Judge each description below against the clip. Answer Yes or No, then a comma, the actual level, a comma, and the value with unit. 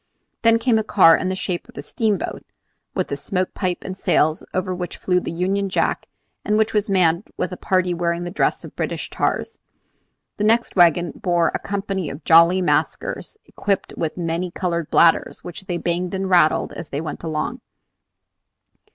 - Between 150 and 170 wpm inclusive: No, average, 185 wpm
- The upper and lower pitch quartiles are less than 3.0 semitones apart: Yes, narrow, 2.6 semitones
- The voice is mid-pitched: Yes, medium, 180 Hz